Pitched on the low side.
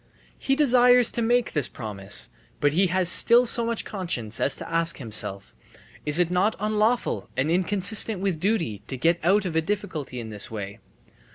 No: medium, 180 Hz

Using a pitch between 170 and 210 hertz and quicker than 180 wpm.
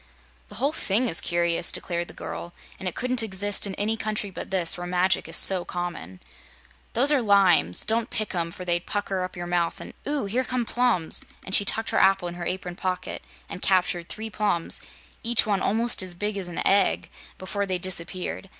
Yes: high, 190 Hz; fast, 205 wpm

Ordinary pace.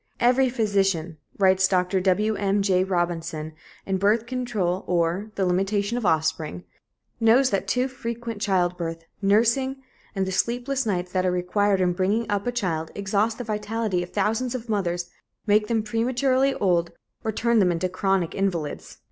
Yes: average, 155 wpm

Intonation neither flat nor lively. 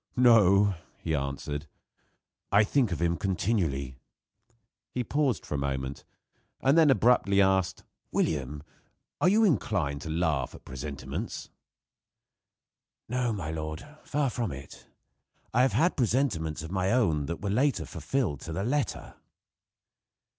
No: wide, 8.2 semitones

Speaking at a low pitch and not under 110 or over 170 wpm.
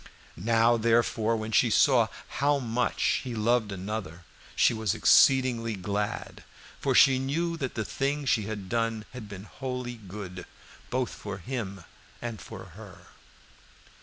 Yes: low, 115 Hz; average, 140 wpm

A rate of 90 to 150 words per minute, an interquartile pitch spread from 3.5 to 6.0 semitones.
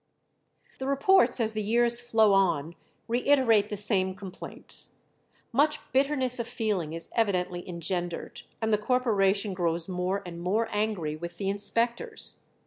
Yes: slow, 135 wpm; average, 4.6 semitones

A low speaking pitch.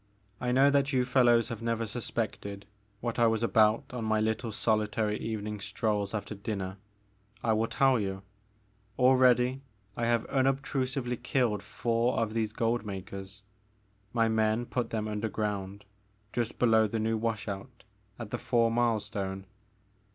Yes: low, 110 Hz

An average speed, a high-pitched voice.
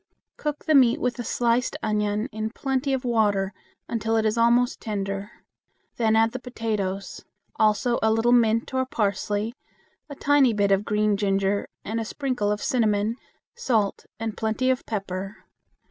Yes: average, 160 wpm; high, 220 Hz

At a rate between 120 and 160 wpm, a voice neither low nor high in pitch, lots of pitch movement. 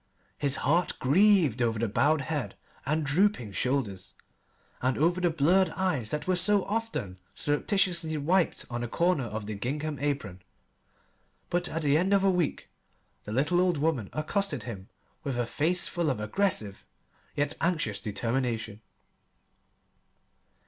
Yes: average, 145 wpm; medium, 145 Hz; wide, 6.7 semitones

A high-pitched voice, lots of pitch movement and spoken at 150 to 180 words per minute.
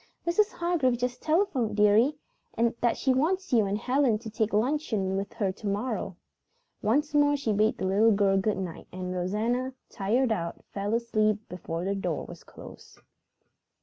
No: high, 220 Hz; average, 4.6 semitones; average, 165 wpm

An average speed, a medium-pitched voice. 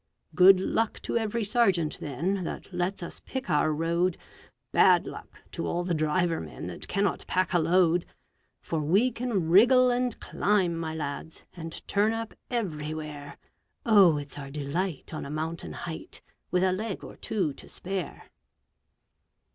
Yes: average, 155 wpm; medium, 175 Hz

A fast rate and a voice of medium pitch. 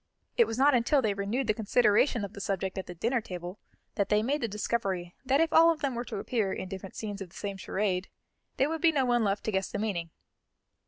No: fast, 250 wpm; high, 210 Hz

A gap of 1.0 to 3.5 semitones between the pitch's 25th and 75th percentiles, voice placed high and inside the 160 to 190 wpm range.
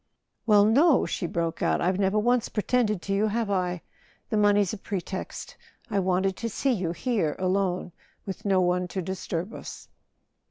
Yes: average, 2.8 semitones; high, 195 Hz; average, 170 wpm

